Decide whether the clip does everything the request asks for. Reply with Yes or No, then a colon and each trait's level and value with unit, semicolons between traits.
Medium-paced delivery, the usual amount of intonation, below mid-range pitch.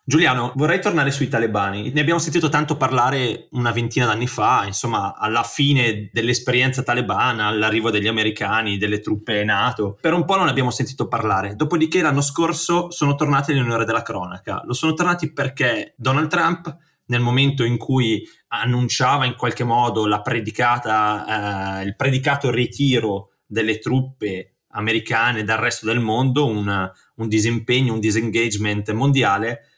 Yes: average, 145 wpm; average, 4.1 semitones; low, 120 Hz